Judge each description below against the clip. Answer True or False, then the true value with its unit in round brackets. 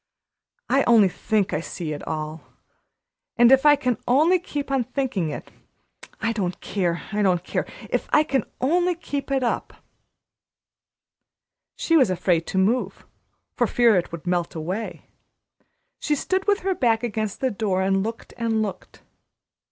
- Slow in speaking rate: False (160 wpm)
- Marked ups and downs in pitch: True (6.6 semitones)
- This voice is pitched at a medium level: False (225 Hz)